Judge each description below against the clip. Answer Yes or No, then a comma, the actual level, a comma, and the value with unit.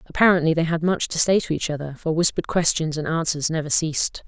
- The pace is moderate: No, fast, 225 wpm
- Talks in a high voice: No, medium, 160 Hz